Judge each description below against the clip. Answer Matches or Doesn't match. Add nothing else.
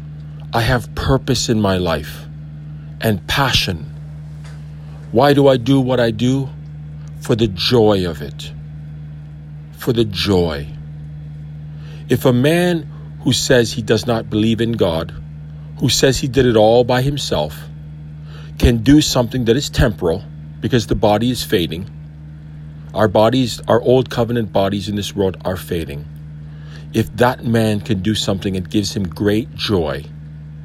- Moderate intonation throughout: Doesn't match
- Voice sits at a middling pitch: Doesn't match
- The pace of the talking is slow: Doesn't match